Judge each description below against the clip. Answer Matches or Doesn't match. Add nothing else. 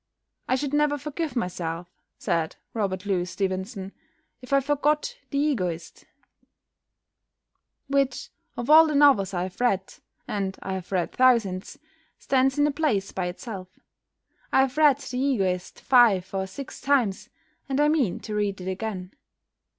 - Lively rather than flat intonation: Matches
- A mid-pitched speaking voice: Doesn't match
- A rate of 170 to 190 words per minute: Doesn't match